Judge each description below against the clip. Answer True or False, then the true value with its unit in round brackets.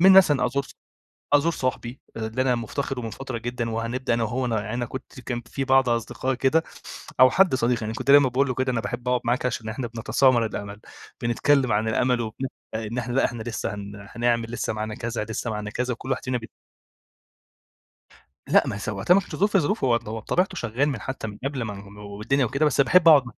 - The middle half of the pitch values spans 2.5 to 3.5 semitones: True (3.0 semitones)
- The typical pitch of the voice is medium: False (120 Hz)